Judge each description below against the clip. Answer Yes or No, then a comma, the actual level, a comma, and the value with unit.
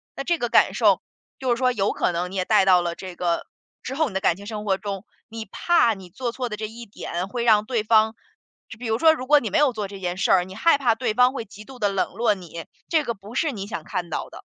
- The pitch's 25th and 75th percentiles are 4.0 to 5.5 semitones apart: Yes, average, 4.4 semitones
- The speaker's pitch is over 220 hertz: No, high, 215 Hz